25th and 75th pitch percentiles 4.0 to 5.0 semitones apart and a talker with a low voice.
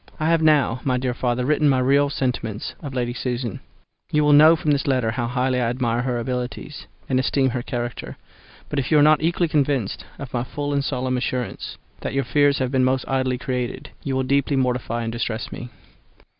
No: narrow, 2.5 semitones; low, 130 Hz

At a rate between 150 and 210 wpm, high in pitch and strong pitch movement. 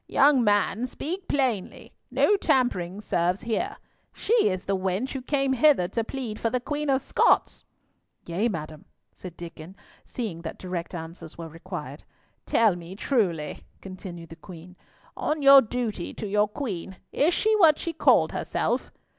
Yes: average, 155 wpm; high, 210 Hz; wide, 7.2 semitones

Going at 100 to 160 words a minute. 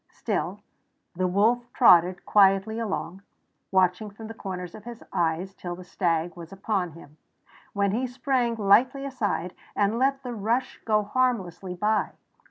Yes: average, 150 wpm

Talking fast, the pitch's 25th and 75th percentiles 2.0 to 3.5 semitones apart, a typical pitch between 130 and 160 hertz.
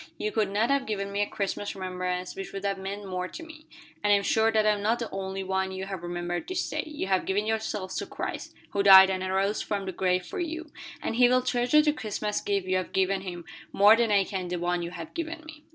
No: fast, 260 wpm; average, 2.9 semitones; high, 200 Hz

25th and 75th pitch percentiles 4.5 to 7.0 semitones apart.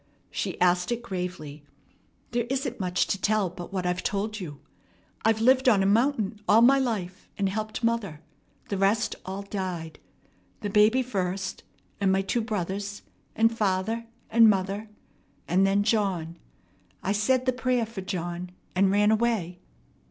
No: average, 3.4 semitones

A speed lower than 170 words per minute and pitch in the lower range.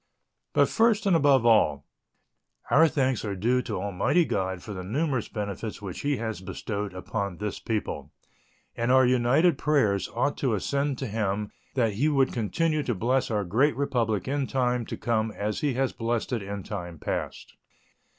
No: average, 175 wpm; low, 115 Hz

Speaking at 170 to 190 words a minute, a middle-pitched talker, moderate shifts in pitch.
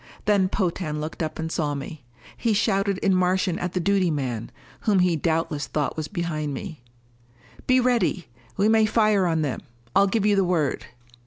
Yes: average, 180 wpm; medium, 180 Hz; average, 4.3 semitones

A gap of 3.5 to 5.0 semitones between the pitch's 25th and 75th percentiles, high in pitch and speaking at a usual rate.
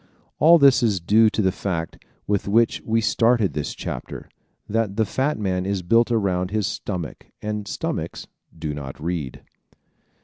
No: average, 4.0 semitones; low, 100 Hz; average, 160 wpm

